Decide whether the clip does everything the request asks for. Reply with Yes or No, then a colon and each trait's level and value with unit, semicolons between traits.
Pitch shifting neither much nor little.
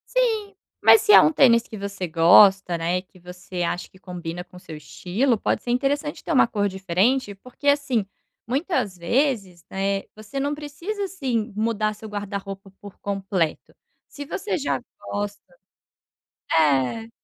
No: wide, 6.8 semitones